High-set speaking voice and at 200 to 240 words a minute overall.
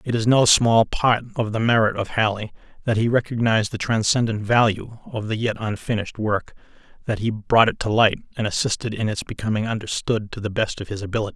No: low, 110 Hz; fast, 205 wpm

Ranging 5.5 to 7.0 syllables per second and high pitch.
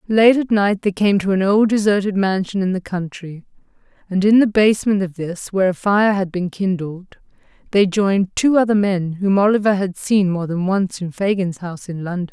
No: 5.2 syllables/s; high, 195 Hz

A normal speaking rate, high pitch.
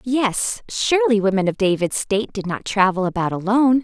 Yes: average, 170 wpm; high, 215 Hz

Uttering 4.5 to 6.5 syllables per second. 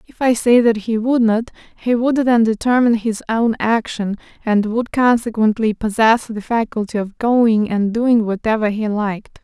Yes: 4.6 syllables/s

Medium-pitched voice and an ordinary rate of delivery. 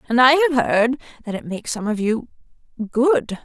No: high, 230 Hz; average, 175 wpm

